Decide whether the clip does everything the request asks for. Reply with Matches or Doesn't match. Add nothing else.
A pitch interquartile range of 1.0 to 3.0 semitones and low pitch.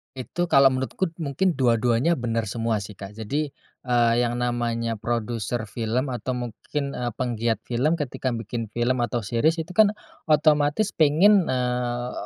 Doesn't match